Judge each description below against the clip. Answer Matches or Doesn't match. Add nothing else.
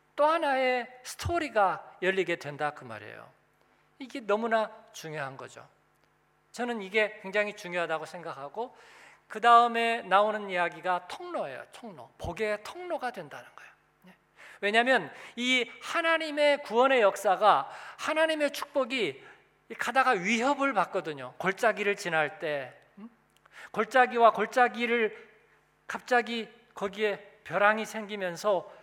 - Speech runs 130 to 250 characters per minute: Doesn't match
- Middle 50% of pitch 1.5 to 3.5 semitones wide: Doesn't match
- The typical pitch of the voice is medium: Doesn't match